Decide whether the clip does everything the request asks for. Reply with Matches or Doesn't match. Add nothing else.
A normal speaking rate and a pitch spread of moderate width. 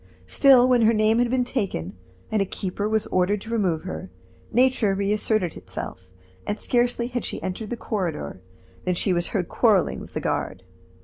Matches